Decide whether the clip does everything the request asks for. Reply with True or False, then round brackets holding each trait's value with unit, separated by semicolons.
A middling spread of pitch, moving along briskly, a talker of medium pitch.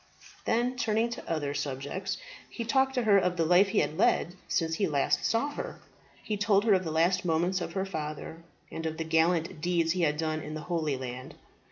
True (3.9 semitones; 215 wpm; 170 Hz)